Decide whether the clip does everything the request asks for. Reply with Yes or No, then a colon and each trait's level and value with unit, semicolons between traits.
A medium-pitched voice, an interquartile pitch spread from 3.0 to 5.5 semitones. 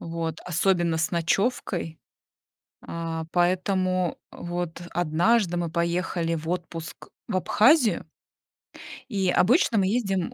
No: medium, 175 Hz; narrow, 2.4 semitones